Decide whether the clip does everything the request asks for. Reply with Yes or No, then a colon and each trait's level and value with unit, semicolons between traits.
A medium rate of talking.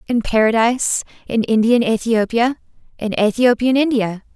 No: slow, 85 wpm